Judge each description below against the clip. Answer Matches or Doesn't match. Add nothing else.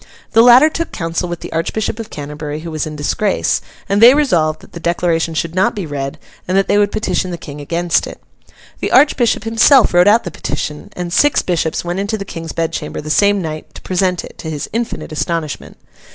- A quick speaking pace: Matches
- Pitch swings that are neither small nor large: Matches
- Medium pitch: Matches